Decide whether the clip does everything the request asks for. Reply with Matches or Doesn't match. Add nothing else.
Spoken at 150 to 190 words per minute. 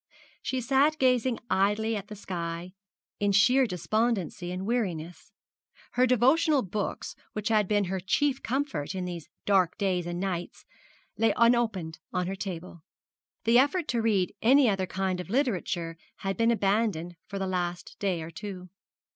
Matches